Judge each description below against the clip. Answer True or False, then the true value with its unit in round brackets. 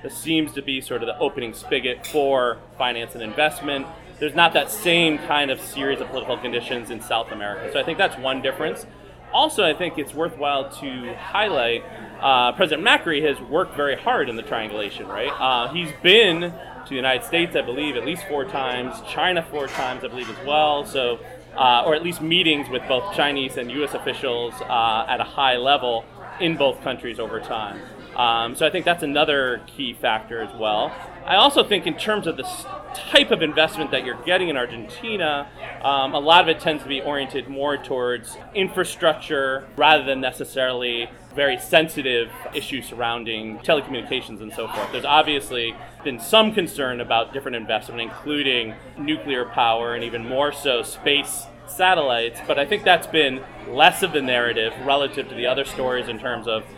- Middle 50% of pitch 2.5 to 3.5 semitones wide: False (4.3 semitones)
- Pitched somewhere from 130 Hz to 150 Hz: True (140 Hz)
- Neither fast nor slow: True (185 wpm)